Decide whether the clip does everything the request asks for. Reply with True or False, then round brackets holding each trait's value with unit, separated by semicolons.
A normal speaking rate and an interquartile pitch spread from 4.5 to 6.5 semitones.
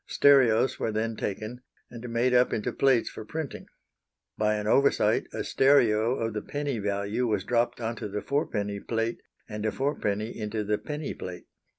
False (170 wpm; 3.0 semitones)